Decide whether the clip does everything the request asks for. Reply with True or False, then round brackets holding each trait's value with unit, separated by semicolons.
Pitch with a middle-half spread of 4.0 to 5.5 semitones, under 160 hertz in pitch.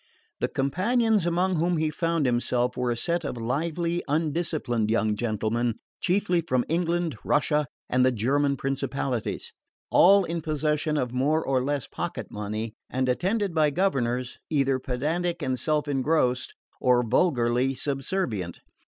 True (5.2 semitones; 140 Hz)